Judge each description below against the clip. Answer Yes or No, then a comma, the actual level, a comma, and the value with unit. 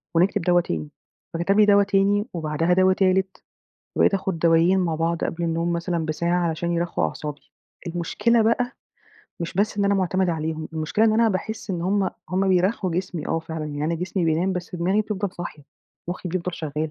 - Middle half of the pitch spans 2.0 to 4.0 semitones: Yes, average, 2.8 semitones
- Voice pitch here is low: No, medium, 175 Hz